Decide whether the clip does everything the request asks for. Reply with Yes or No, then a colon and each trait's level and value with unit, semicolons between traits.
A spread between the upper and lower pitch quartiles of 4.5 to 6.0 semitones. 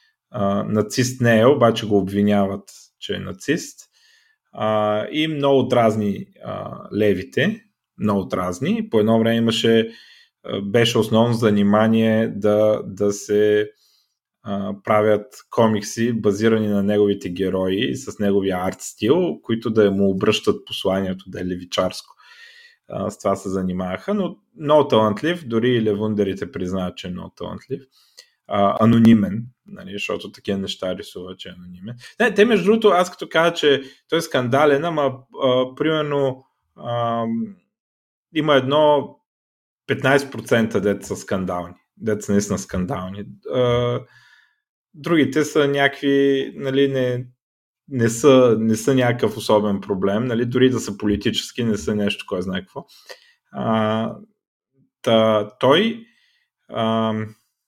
Yes: average, 5.3 semitones